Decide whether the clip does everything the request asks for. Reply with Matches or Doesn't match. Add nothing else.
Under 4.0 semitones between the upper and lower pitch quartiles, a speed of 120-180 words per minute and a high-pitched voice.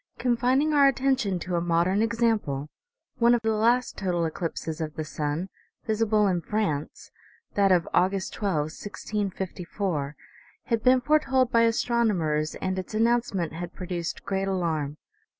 Doesn't match